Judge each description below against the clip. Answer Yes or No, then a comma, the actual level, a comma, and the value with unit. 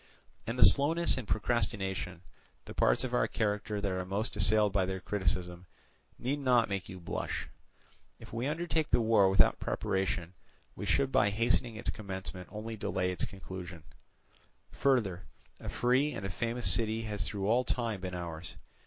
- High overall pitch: No, low, 105 Hz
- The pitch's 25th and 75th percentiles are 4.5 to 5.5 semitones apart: No, average, 4.1 semitones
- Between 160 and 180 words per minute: Yes, average, 165 wpm